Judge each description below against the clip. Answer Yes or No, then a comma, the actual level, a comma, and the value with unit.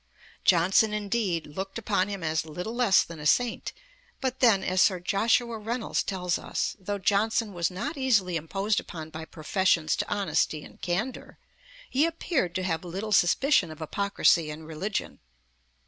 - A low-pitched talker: No, high, 190 Hz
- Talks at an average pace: Yes, average, 160 wpm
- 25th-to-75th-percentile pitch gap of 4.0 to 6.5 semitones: Yes, average, 4.5 semitones